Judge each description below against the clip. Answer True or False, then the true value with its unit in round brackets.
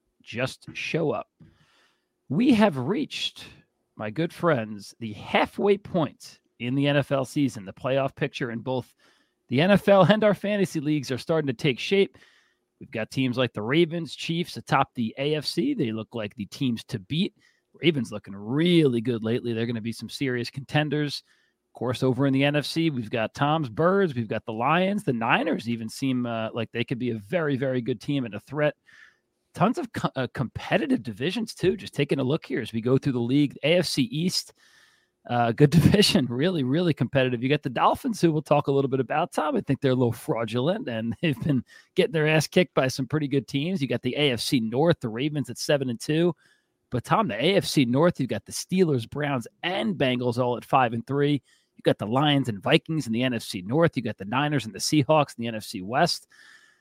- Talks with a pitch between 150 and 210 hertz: False (140 Hz)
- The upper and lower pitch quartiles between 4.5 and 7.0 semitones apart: True (5.2 semitones)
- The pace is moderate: False (210 wpm)